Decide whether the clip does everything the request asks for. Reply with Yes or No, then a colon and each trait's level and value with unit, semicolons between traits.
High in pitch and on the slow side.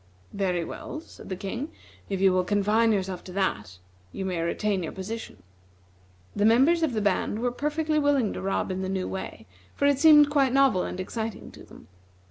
No: high, 210 Hz; average, 195 wpm